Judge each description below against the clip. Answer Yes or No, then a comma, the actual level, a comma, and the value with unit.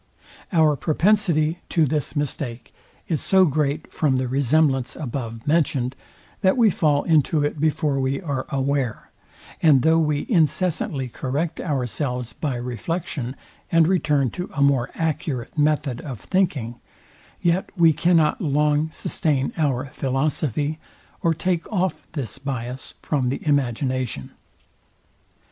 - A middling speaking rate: No, slow, 125 wpm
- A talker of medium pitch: Yes, medium, 145 Hz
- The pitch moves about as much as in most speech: Yes, average, 3.4 semitones